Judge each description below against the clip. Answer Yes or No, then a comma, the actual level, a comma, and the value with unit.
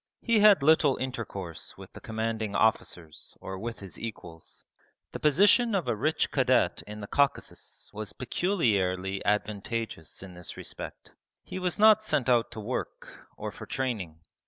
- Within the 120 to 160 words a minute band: Yes, average, 155 wpm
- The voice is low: Yes, low, 115 Hz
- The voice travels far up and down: Yes, wide, 6.7 semitones